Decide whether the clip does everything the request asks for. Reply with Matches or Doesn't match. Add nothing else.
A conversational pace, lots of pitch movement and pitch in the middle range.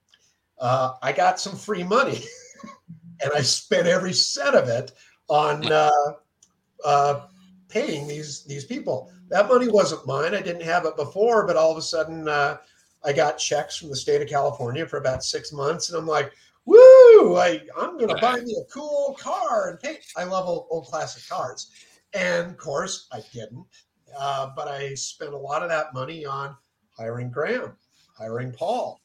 Matches